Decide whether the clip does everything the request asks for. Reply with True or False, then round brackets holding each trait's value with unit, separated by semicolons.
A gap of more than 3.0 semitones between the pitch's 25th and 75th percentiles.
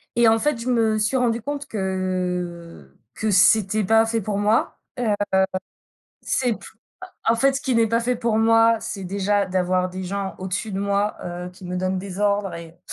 True (3.5 semitones)